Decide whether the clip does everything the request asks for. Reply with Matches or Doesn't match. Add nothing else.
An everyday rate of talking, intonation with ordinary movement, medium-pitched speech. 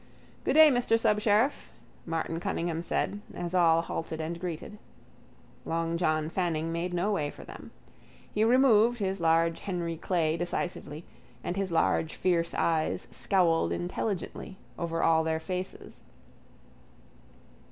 Doesn't match